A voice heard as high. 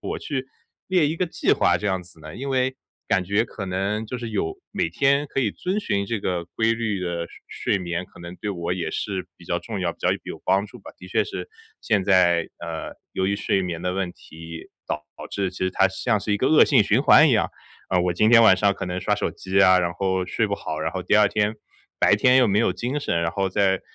No: very low, 95 Hz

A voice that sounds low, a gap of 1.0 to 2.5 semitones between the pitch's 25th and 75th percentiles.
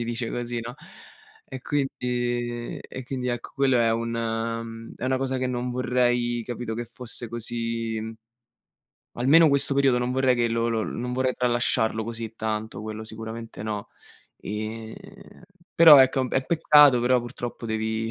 Yes: low, 120 Hz; narrow, 2.0 semitones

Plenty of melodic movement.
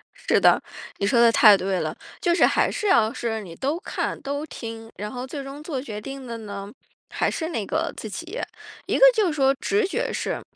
Yes: wide, 6.6 semitones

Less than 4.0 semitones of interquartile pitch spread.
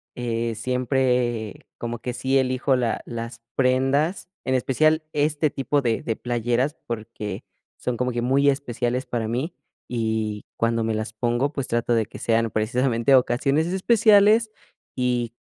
Yes: average, 2.8 semitones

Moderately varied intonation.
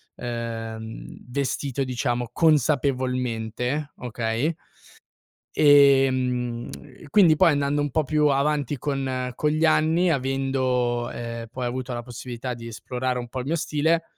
Yes: average, 3.2 semitones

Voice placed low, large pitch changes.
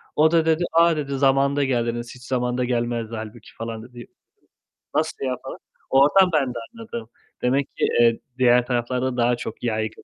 No: low, 125 Hz; average, 2.8 semitones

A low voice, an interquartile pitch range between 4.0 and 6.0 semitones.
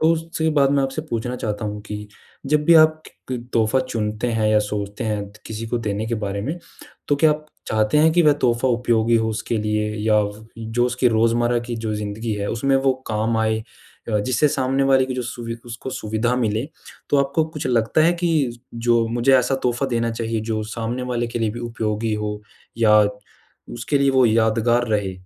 No: low, 115 Hz; average, 3.3 semitones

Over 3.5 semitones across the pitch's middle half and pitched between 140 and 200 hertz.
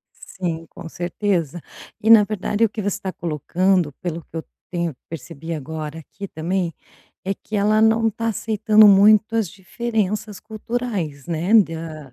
Yes: average, 4.6 semitones; high, 190 Hz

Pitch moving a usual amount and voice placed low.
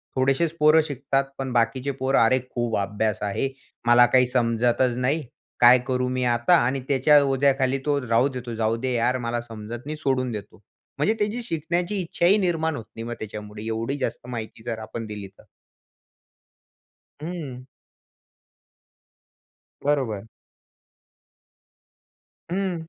Yes: average, 3.7 semitones; low, 125 Hz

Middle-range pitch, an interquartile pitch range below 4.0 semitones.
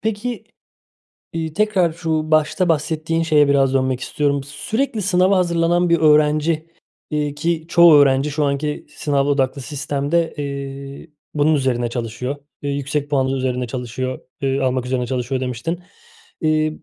Yes: medium, 145 Hz; average, 3.4 semitones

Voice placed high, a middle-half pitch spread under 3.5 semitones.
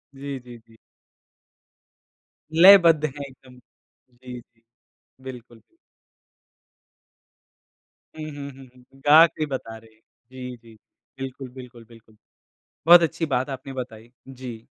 No: low, 130 Hz; average, 2.9 semitones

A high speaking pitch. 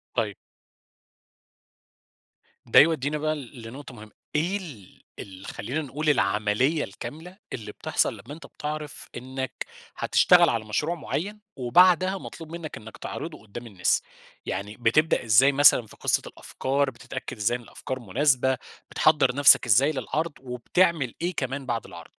No: low, 135 Hz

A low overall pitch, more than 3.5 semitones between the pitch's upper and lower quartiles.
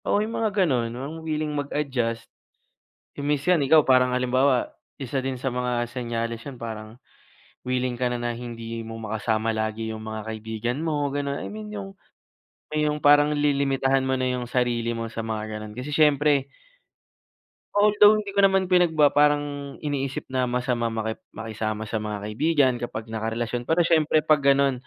Yes: low, 130 Hz; average, 4.2 semitones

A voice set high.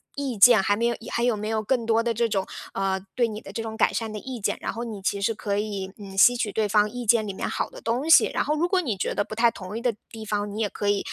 Yes: high, 220 Hz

